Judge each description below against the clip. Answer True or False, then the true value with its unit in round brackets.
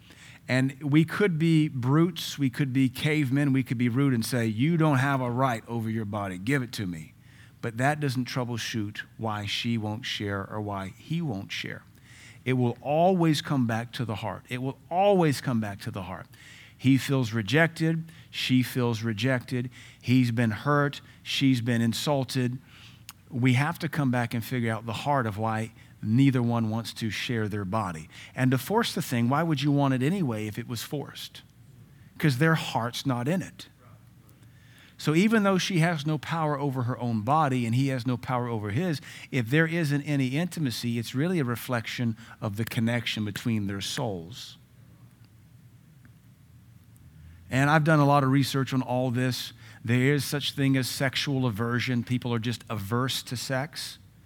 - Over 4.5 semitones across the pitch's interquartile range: False (3.6 semitones)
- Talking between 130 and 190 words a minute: True (180 wpm)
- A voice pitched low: True (125 Hz)